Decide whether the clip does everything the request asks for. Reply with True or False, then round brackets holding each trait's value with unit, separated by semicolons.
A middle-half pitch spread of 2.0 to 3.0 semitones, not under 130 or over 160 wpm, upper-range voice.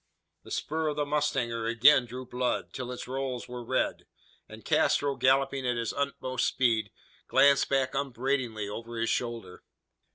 False (2.6 semitones; 155 wpm; 130 Hz)